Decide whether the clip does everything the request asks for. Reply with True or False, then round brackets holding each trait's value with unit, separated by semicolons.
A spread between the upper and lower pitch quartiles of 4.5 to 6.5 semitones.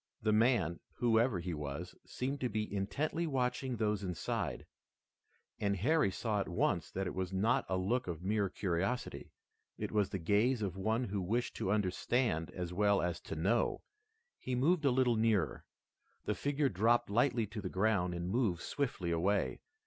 True (4.9 semitones)